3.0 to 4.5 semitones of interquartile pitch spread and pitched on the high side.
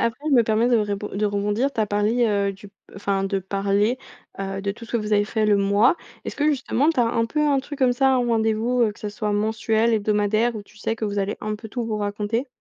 No: narrow, 2.4 semitones; high, 215 Hz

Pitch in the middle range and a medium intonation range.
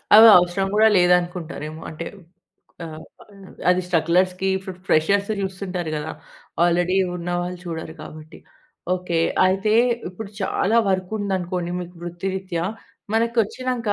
No: medium, 180 Hz; narrow, 2.0 semitones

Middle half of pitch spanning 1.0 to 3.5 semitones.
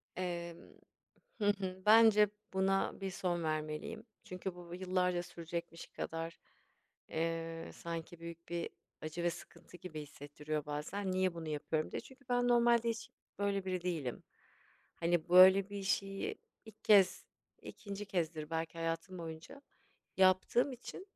Yes: average, 3.0 semitones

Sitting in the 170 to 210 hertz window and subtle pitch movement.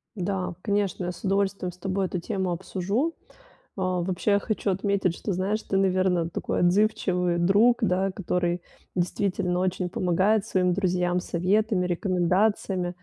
Yes: medium, 185 Hz; narrow, 1.9 semitones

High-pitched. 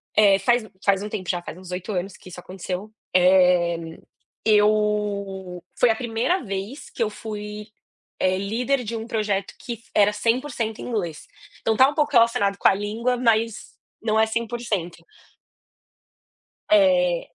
Yes: high, 210 Hz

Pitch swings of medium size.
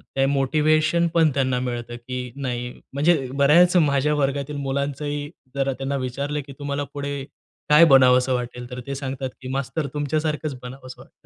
No: narrow, 2.3 semitones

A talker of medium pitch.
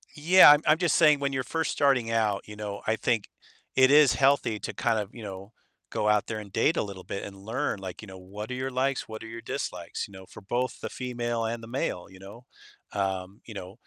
No: low, 115 Hz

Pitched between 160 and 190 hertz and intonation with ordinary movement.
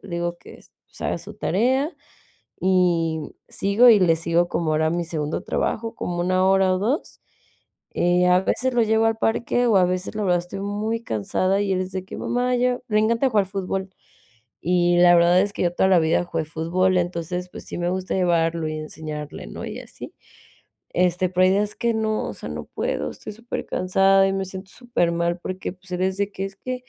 Yes: medium, 185 Hz; average, 3.1 semitones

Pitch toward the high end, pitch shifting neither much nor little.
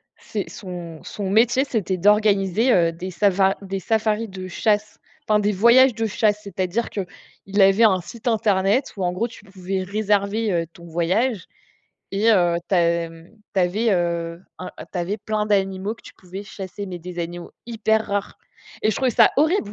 Yes: high, 195 Hz; average, 3.1 semitones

